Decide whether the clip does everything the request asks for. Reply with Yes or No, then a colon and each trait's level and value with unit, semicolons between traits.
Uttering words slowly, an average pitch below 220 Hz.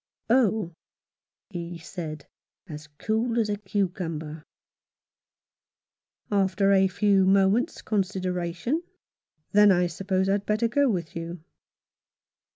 Yes: slow, 105 wpm; high, 190 Hz